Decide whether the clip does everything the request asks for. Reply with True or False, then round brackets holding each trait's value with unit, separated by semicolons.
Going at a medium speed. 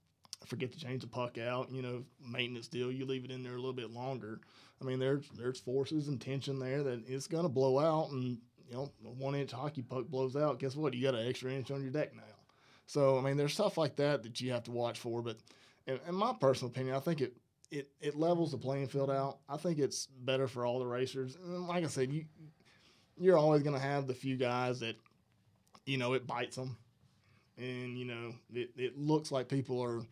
False (240 wpm)